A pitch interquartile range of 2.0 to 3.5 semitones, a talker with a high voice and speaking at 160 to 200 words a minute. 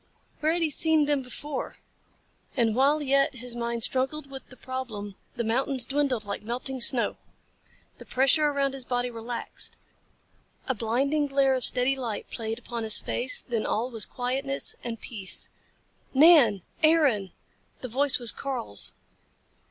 No: average, 2.9 semitones; very high, 255 Hz; average, 150 wpm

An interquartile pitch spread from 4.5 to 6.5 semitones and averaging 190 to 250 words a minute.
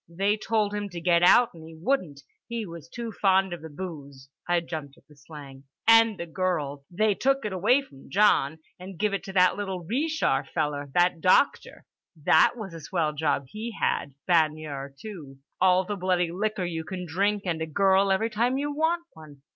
Yes: average, 4.8 semitones; average, 200 wpm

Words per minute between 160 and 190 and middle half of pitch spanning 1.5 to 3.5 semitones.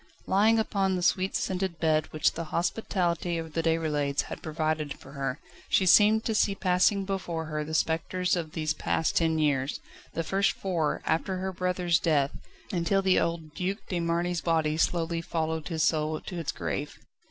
Yes: average, 175 wpm; average, 2.8 semitones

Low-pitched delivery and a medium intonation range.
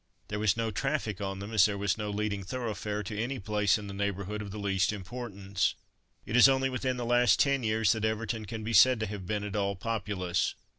No: low, 105 Hz; narrow, 2.3 semitones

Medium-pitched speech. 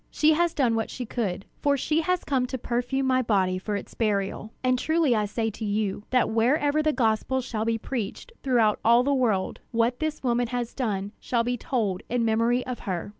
No: high, 240 Hz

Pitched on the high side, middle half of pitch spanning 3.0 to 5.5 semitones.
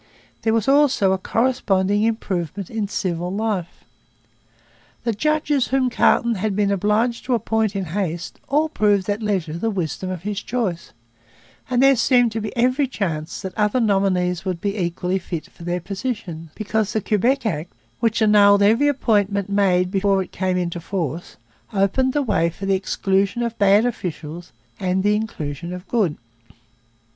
Yes: high, 200 Hz; average, 3.7 semitones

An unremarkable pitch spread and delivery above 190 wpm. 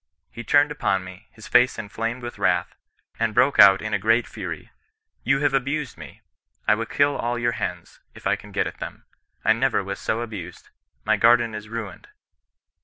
Yes: average, 3.0 semitones; average, 200 wpm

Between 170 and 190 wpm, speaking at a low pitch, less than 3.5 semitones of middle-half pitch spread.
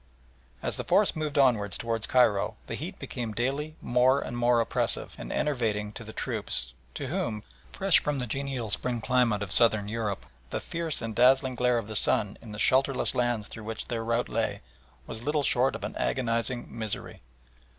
Yes: average, 185 wpm; low, 120 Hz; average, 3.0 semitones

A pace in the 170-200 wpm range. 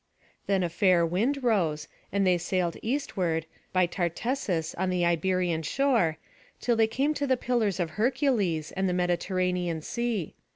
No: average, 155 wpm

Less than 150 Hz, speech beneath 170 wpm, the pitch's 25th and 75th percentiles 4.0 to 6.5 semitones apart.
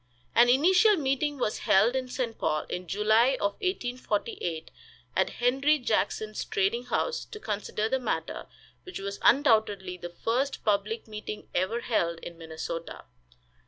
No: high, 225 Hz; average, 140 wpm; average, 4.9 semitones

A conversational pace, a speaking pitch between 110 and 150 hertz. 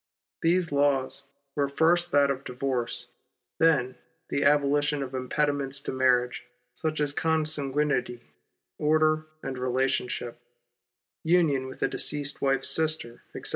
No: slow, 120 wpm; medium, 140 Hz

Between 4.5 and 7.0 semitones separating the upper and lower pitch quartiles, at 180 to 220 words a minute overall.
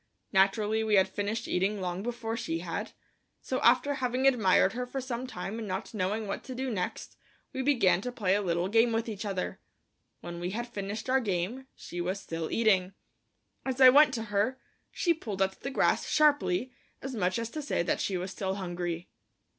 Yes: average, 4.8 semitones; average, 200 wpm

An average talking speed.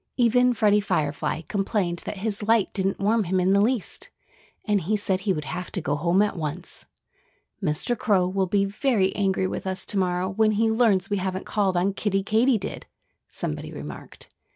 Yes: average, 185 wpm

